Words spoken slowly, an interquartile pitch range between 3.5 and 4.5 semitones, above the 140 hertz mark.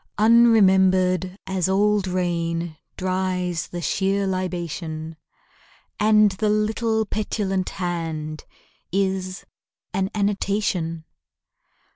No: slow, 80 wpm; average, 2.7 semitones; medium, 185 Hz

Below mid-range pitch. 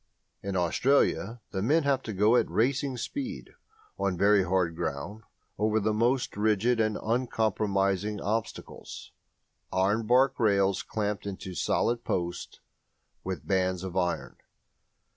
Yes: low, 105 Hz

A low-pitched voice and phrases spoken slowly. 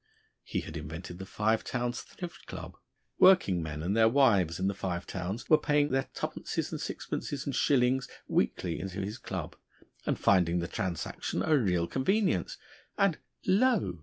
No: low, 105 Hz; average, 165 wpm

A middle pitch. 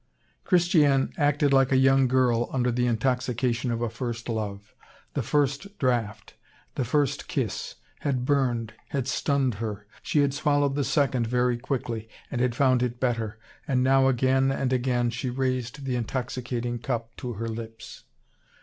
No: low, 125 Hz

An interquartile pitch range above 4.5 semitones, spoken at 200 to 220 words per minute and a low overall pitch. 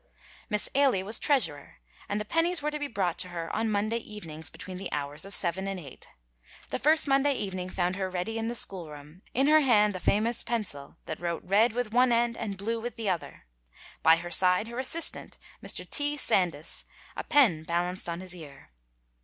No: average, 5.3 semitones; fast, 205 wpm; high, 200 Hz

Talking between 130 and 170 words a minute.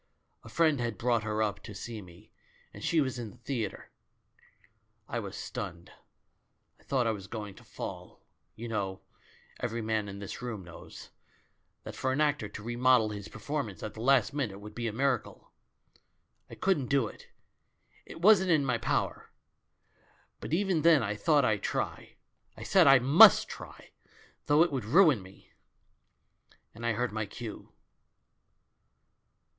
Yes: average, 165 wpm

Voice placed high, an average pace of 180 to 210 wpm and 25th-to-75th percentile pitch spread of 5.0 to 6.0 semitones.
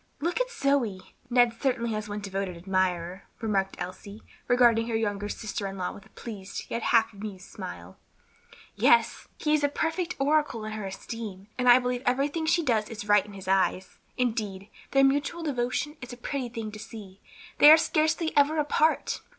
Yes: high, 225 Hz; average, 190 wpm; wide, 5.5 semitones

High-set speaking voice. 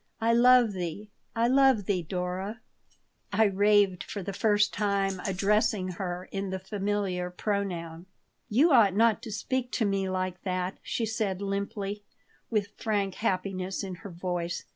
Yes: high, 200 Hz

